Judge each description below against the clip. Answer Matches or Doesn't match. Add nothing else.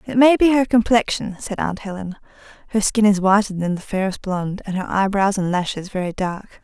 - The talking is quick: Matches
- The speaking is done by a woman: Matches